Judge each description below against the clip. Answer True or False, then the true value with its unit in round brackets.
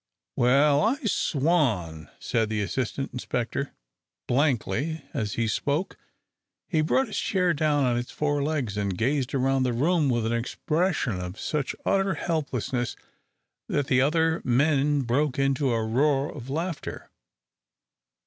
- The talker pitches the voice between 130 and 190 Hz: True (135 Hz)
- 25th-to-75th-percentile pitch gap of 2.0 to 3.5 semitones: False (4.2 semitones)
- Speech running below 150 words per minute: True (140 wpm)